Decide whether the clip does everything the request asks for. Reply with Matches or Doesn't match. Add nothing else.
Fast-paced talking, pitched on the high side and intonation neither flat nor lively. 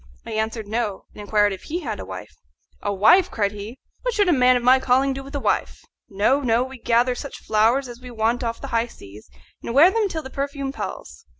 Matches